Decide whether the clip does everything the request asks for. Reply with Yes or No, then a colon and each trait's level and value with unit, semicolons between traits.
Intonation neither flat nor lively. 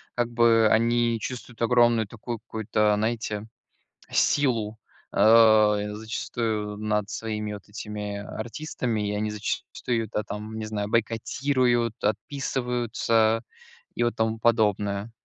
No: narrow, 1.9 semitones